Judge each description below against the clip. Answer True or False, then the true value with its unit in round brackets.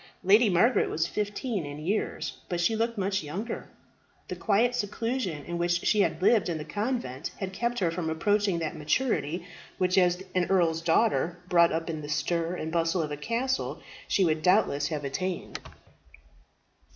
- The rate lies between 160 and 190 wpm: True (175 wpm)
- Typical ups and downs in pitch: True (4.3 semitones)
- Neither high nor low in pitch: True (180 Hz)